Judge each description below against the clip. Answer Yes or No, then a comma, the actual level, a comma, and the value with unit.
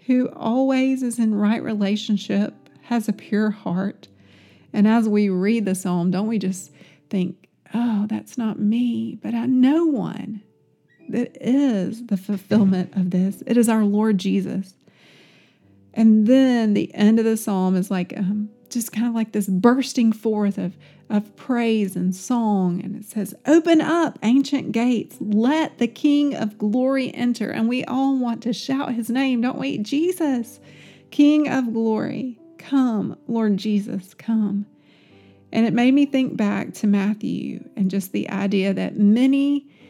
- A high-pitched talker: Yes, high, 220 Hz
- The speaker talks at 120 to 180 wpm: Yes, average, 160 wpm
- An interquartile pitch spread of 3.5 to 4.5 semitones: Yes, average, 3.8 semitones